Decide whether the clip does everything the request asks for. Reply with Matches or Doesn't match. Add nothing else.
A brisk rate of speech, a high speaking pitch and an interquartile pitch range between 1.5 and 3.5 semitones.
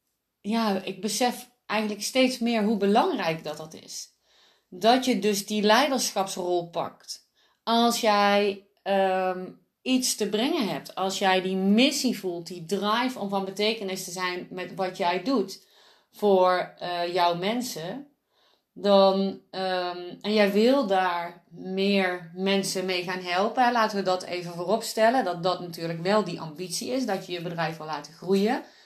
Doesn't match